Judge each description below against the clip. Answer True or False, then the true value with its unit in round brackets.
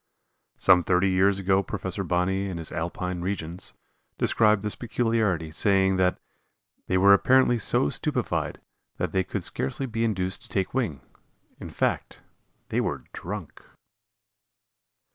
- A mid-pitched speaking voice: False (95 Hz)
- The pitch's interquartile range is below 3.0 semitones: True (2.6 semitones)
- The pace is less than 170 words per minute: True (135 wpm)